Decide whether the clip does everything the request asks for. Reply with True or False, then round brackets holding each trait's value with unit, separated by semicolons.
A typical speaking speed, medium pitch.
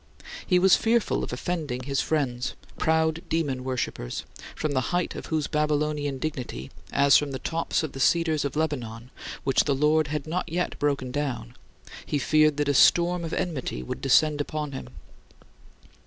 True (170 wpm; 150 Hz)